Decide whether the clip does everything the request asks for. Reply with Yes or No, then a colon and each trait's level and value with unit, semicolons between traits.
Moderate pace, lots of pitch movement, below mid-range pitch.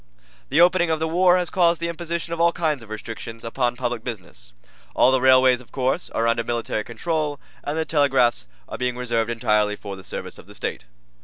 No: fast, 210 wpm; wide, 5.9 semitones; low, 130 Hz